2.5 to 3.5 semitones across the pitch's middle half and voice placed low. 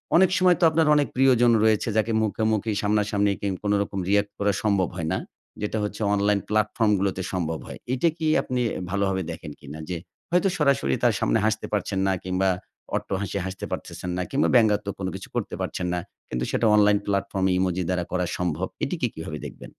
Yes: average, 3.0 semitones; low, 100 Hz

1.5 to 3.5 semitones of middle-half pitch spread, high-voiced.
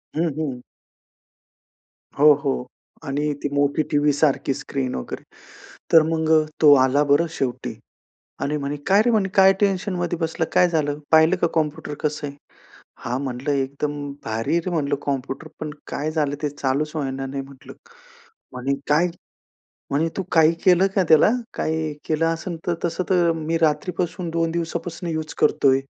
No: average, 2.9 semitones; medium, 155 Hz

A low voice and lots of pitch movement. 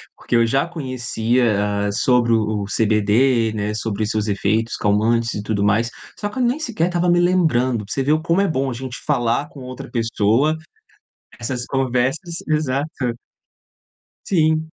Yes: low, 125 Hz; wide, 5.8 semitones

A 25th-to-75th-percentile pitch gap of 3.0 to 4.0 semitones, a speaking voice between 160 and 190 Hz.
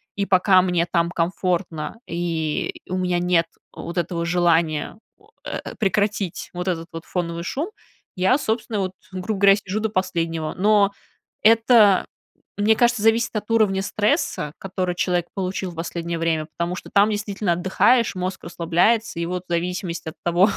Yes: average, 3.4 semitones; medium, 185 Hz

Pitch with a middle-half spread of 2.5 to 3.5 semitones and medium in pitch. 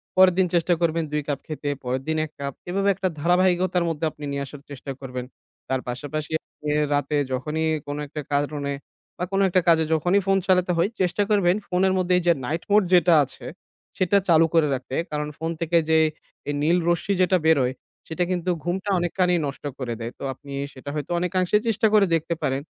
No: average, 4.0 semitones; medium, 165 Hz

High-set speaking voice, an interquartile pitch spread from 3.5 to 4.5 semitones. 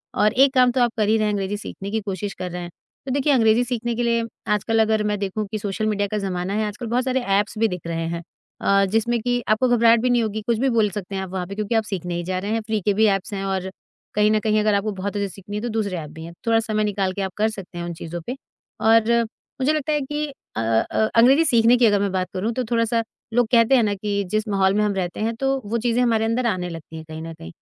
No: high, 215 Hz; average, 3.1 semitones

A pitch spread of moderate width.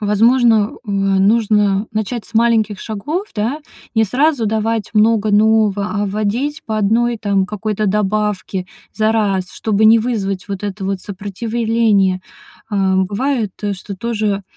No: narrow, 2.2 semitones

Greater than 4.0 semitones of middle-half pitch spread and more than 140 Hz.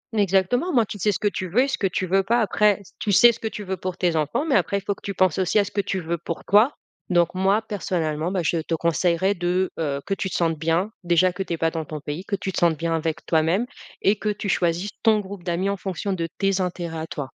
No: average, 3.2 semitones; medium, 185 Hz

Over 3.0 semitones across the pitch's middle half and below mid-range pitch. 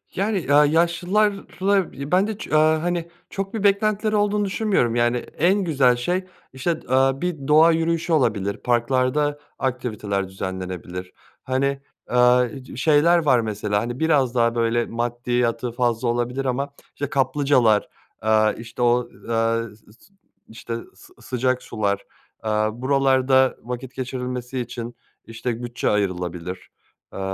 Yes: average, 5.2 semitones; low, 125 Hz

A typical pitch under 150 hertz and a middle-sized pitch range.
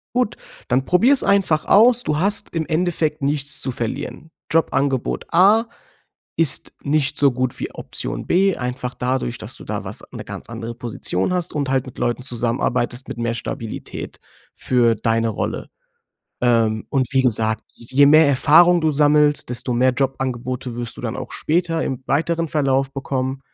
Yes: low, 135 Hz; average, 4.3 semitones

